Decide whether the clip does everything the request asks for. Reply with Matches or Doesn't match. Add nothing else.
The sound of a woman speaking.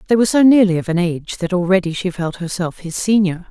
Matches